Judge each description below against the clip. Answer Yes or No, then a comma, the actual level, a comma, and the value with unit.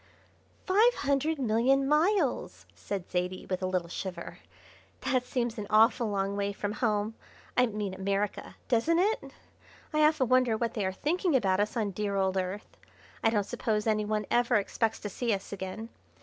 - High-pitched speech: Yes, high, 215 Hz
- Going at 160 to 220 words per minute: Yes, average, 180 wpm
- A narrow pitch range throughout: No, average, 4.3 semitones